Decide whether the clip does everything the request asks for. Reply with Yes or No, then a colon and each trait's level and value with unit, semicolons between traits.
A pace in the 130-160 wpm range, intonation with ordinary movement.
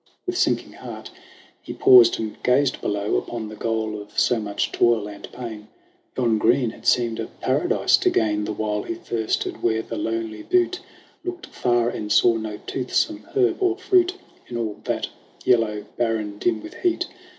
No: average, 175 wpm; average, 3.8 semitones